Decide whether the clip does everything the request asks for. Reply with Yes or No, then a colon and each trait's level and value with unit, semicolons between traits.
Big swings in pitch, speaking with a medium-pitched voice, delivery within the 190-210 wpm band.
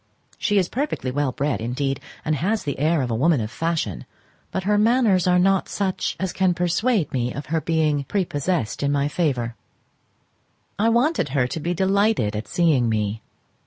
No: wide, 6.3 semitones; medium, 160 Hz; average, 180 wpm